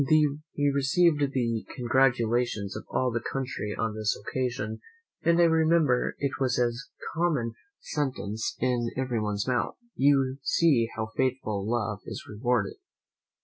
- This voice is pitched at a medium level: No, low, 125 Hz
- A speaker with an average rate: No, slow, 130 wpm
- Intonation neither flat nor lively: Yes, average, 3.5 semitones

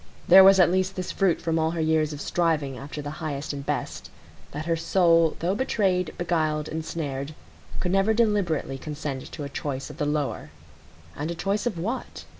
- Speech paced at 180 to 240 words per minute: Yes, average, 185 wpm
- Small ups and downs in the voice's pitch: No, average, 3.6 semitones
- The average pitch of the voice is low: No, medium, 160 Hz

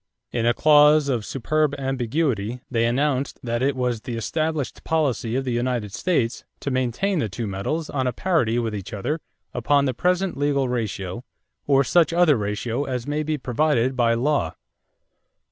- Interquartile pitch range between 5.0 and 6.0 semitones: No, average, 4.2 semitones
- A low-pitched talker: Yes, low, 130 Hz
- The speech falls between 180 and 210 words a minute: No, average, 170 wpm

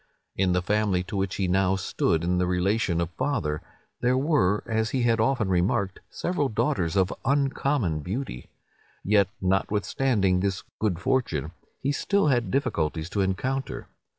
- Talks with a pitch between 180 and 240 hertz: No, low, 100 Hz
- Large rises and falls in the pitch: Yes, wide, 5.7 semitones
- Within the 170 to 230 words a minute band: No, average, 150 wpm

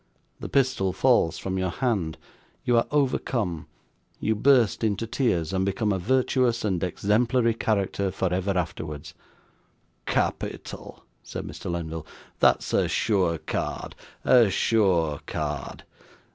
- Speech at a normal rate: No, slow, 125 wpm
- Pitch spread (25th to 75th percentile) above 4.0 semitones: Yes, average, 5.2 semitones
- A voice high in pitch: No, low, 100 Hz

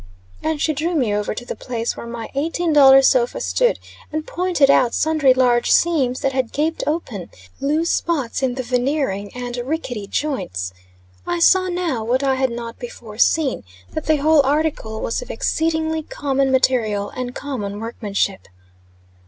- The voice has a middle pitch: No, very high, 265 Hz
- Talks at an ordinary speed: Yes, average, 165 wpm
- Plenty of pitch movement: No, average, 4.9 semitones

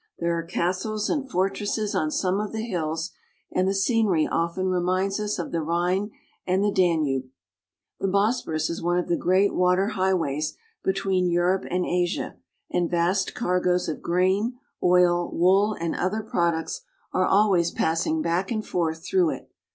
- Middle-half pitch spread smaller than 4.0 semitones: Yes, narrow, 2.6 semitones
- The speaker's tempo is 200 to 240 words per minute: No, average, 160 wpm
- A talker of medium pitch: Yes, medium, 180 Hz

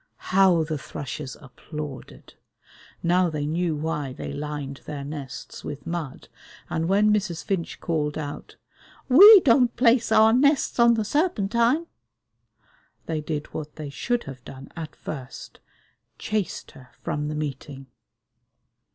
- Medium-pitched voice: Yes, medium, 160 Hz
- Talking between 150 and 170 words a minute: No, slow, 135 wpm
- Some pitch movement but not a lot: No, wide, 6.5 semitones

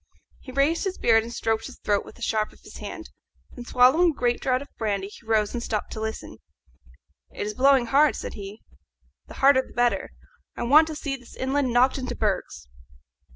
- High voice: Yes, high, 245 Hz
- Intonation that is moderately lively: Yes, average, 3.7 semitones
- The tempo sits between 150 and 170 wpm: No, fast, 205 wpm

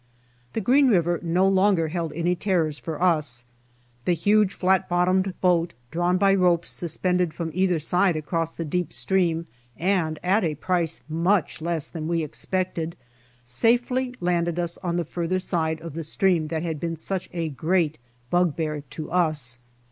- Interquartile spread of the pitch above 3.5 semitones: No, narrow, 2.4 semitones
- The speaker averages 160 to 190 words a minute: Yes, average, 165 wpm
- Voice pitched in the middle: Yes, medium, 170 Hz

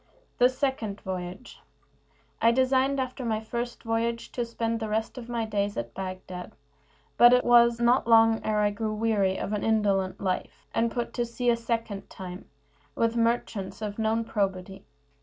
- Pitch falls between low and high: No, high, 225 Hz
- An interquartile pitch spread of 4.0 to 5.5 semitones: No, average, 2.8 semitones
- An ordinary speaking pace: Yes, average, 175 wpm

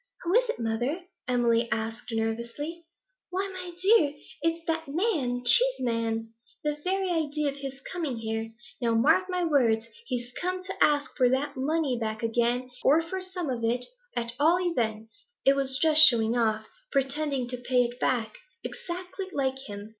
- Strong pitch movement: Yes, wide, 6.1 semitones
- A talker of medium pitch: No, very high, 270 Hz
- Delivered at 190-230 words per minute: No, average, 165 wpm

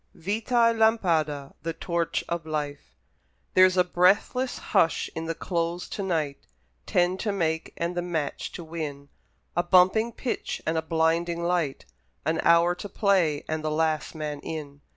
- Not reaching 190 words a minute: Yes, average, 160 wpm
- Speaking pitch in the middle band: Yes, medium, 170 Hz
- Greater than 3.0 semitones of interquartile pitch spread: No, narrow, 2.6 semitones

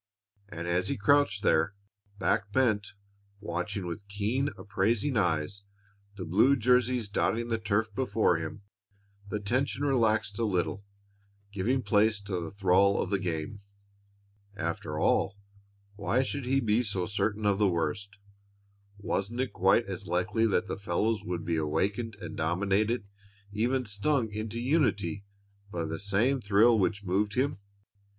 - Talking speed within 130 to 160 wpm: Yes, average, 145 wpm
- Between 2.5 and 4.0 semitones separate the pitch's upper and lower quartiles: Yes, average, 3.1 semitones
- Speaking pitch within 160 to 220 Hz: No, low, 105 Hz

